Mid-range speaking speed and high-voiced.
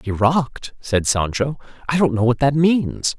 No: average, 170 wpm; low, 130 Hz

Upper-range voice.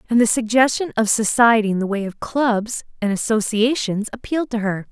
Yes: high, 225 Hz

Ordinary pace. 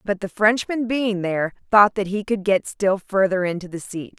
No: fast, 215 wpm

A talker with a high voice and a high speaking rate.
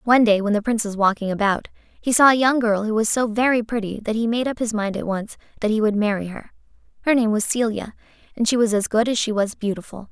Yes: high, 220 Hz; fast, 260 wpm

